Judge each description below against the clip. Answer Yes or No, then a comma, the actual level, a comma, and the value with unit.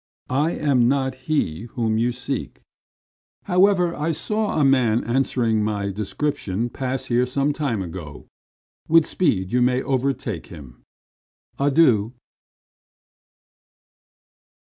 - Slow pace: Yes, slow, 110 wpm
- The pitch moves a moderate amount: Yes, average, 4.6 semitones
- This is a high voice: No, low, 125 Hz